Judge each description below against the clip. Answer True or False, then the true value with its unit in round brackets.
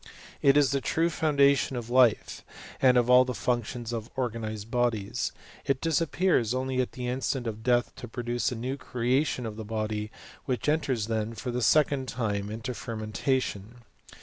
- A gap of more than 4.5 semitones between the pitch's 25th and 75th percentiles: False (2.8 semitones)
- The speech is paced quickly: False (175 wpm)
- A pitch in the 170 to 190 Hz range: False (125 Hz)